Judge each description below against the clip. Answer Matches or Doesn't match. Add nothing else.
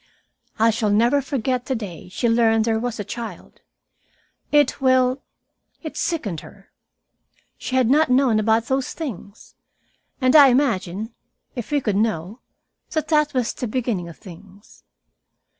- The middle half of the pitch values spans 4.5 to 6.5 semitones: Doesn't match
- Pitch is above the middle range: Matches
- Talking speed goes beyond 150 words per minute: Doesn't match